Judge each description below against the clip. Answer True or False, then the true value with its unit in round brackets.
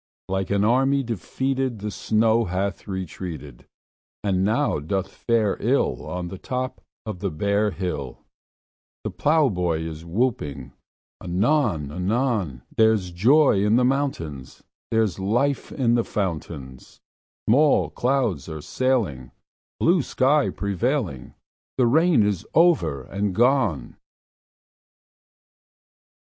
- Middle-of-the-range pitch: False (105 Hz)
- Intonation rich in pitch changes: True (6.5 semitones)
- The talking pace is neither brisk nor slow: False (110 wpm)